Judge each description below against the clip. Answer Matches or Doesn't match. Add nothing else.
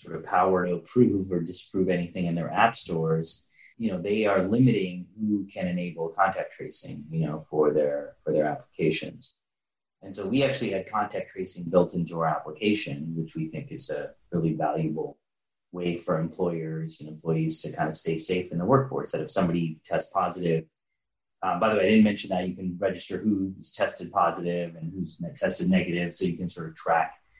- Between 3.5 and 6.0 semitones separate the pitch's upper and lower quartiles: Doesn't match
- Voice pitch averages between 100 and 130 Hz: Doesn't match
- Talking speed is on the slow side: Doesn't match